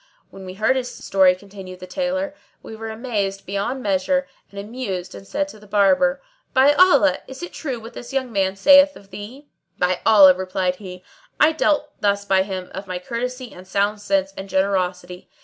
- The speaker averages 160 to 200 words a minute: Yes, average, 190 wpm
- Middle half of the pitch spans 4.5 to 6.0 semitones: Yes, wide, 5.4 semitones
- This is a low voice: No, high, 200 Hz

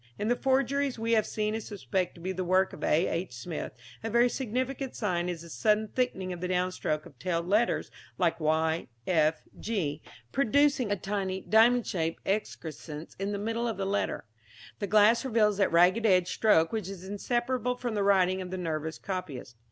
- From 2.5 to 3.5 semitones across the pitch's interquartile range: No, average, 4.5 semitones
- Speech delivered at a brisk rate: No, average, 190 wpm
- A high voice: Yes, high, 195 Hz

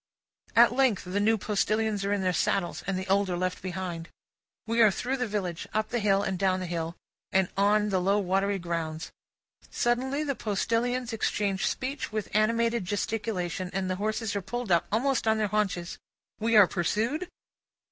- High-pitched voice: Yes, high, 205 Hz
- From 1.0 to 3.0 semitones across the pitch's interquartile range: No, average, 3.4 semitones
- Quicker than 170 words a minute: Yes, average, 180 wpm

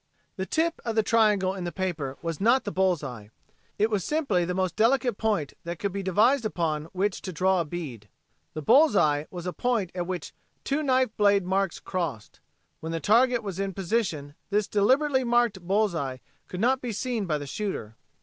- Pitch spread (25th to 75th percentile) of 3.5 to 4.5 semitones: No, average, 5.0 semitones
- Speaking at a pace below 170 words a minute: No, average, 200 wpm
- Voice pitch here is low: No, high, 195 Hz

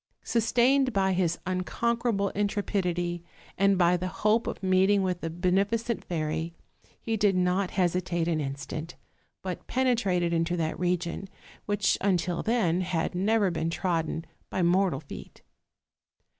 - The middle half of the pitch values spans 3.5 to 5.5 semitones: No, average, 2.9 semitones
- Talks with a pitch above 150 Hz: Yes, medium, 185 Hz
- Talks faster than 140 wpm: No, slow, 135 wpm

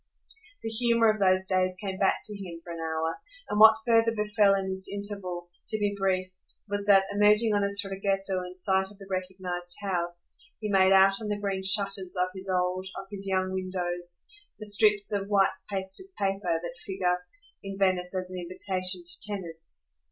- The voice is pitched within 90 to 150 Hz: No, high, 190 Hz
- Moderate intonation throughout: No, narrow, 1.8 semitones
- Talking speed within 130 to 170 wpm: No, average, 190 wpm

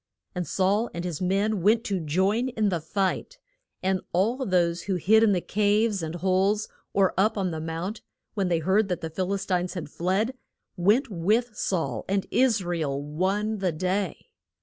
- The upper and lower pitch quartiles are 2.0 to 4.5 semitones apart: Yes, average, 3.2 semitones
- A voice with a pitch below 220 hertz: Yes, high, 190 Hz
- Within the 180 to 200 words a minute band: Yes, average, 190 wpm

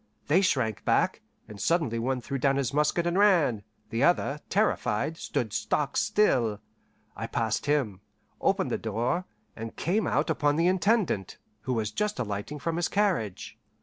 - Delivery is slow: No, average, 160 wpm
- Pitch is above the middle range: No, medium, 140 Hz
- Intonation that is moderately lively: No, wide, 7.4 semitones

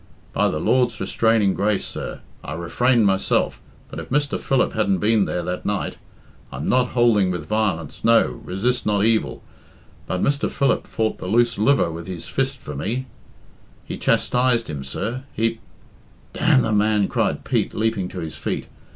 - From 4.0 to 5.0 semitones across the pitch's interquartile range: Yes, average, 4.6 semitones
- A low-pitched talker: Yes, low, 110 Hz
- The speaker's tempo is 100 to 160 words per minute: No, average, 175 wpm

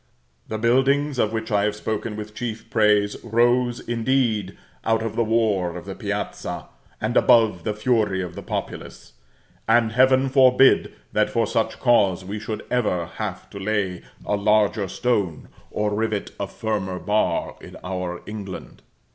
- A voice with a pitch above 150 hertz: No, low, 110 Hz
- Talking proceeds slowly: No, average, 155 wpm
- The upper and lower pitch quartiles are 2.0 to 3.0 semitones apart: Yes, average, 2.7 semitones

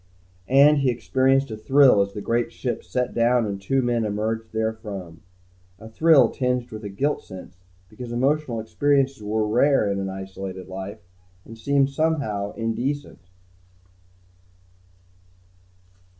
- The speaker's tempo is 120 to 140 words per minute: Yes, slow, 135 wpm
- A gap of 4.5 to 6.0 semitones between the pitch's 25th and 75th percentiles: Yes, average, 4.8 semitones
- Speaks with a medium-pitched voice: No, low, 115 Hz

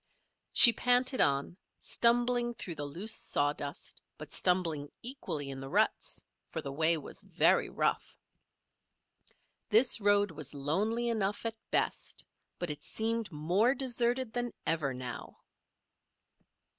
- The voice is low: No, high, 200 Hz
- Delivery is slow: Yes, slow, 125 wpm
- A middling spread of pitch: No, wide, 8.2 semitones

